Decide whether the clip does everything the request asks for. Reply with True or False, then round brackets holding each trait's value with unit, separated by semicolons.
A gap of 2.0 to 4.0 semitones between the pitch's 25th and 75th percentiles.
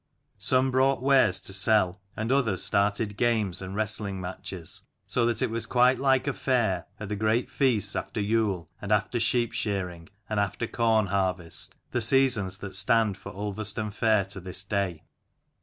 True (3.3 semitones)